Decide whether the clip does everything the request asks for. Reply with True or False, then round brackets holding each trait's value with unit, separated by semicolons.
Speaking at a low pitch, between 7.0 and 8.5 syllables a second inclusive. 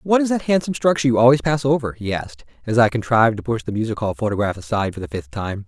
True (120 Hz; 7.3 syllables/s)